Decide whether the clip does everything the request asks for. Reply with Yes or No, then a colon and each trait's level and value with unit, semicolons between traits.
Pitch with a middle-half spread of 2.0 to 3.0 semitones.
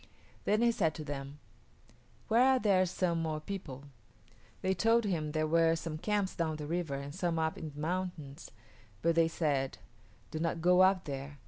No: average, 3.4 semitones